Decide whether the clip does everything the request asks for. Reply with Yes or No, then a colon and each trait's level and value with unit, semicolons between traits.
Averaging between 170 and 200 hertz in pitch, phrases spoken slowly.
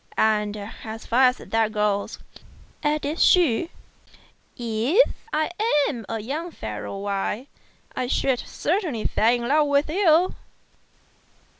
No: high, 245 Hz; slow, 120 wpm